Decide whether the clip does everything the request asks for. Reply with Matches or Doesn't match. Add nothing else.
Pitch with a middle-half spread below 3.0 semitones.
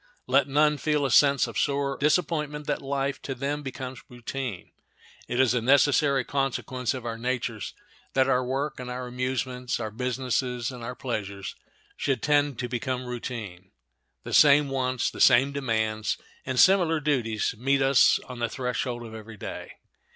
Matches